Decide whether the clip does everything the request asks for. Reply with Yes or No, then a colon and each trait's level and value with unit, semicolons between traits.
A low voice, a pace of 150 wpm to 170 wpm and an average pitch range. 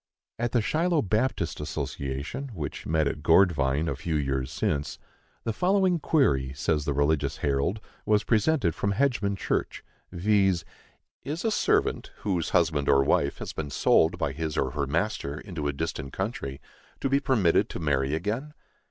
No: very low, 85 Hz; average, 160 wpm; wide, 7.6 semitones